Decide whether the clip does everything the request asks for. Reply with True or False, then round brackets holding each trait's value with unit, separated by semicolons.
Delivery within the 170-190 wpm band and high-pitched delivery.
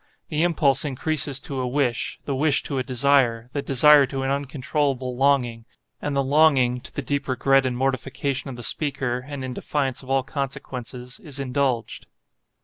False (175 wpm; 135 Hz)